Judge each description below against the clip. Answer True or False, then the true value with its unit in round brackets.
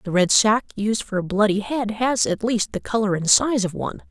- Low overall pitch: False (215 Hz)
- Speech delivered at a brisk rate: True (250 wpm)